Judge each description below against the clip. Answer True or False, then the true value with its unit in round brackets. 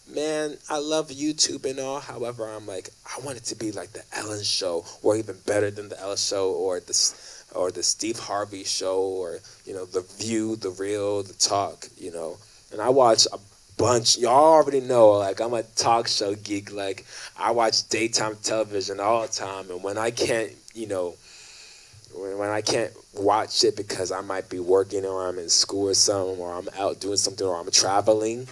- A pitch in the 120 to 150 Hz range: False (105 Hz)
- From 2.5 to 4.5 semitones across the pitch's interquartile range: False (5.4 semitones)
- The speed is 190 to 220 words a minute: True (200 wpm)